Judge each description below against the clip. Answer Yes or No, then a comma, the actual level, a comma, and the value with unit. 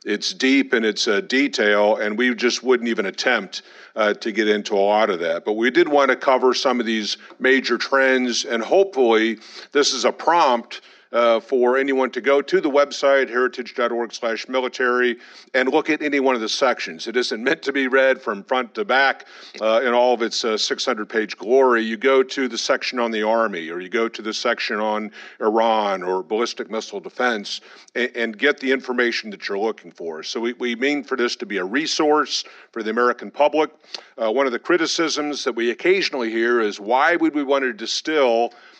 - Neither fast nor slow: No, fast, 210 wpm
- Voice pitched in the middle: No, low, 125 Hz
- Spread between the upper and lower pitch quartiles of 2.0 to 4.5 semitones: Yes, average, 3.3 semitones